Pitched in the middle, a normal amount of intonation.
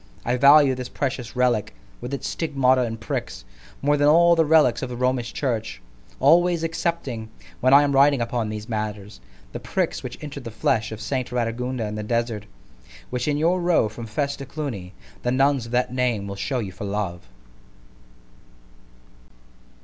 No: low, 125 Hz; average, 4.3 semitones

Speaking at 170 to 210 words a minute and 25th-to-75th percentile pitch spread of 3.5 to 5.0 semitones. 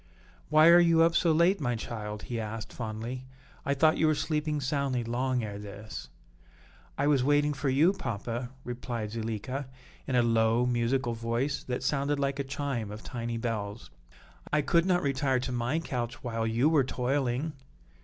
Yes: average, 175 wpm; average, 3.9 semitones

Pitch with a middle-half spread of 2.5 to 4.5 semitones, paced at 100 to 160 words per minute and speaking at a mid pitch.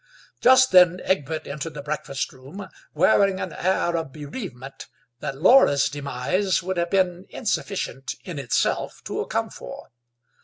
No: average, 5.1 semitones; average, 140 wpm; medium, 170 Hz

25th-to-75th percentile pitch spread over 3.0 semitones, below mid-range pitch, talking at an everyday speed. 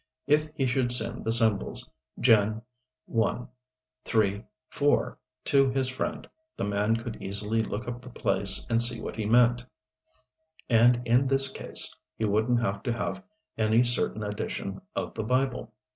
No: narrow, 2.4 semitones; low, 115 Hz; average, 155 wpm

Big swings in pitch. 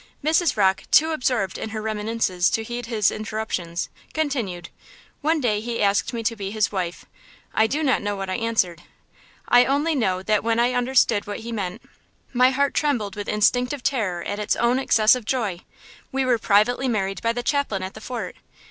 No: average, 3.7 semitones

